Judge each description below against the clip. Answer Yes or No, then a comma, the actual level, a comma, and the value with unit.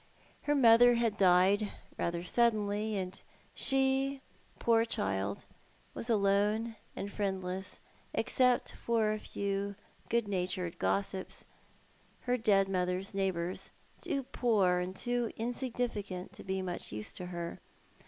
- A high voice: Yes, high, 200 Hz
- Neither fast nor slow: No, slow, 125 wpm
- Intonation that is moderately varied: Yes, average, 4.0 semitones